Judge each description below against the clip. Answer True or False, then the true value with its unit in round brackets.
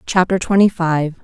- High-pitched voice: False (175 Hz)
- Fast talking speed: False (145 wpm)